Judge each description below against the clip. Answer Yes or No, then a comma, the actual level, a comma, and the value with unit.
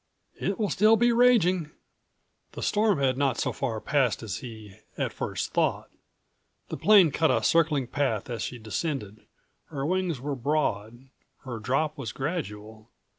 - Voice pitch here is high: No, medium, 140 Hz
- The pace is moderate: Yes, average, 155 wpm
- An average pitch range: No, wide, 6.6 semitones